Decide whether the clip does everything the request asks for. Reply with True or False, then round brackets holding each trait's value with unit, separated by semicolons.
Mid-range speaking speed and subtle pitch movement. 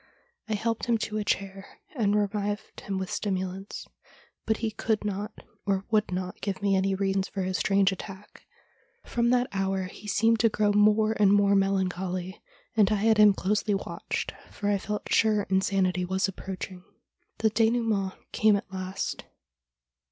True (165 wpm; 1.9 semitones)